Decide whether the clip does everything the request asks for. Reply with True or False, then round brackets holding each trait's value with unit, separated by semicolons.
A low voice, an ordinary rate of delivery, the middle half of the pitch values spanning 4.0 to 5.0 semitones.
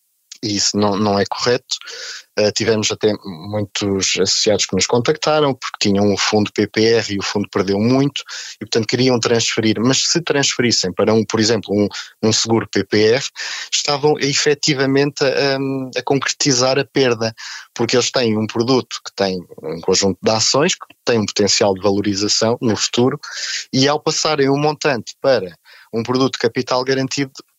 True (115 Hz; 170 wpm; 4.5 semitones)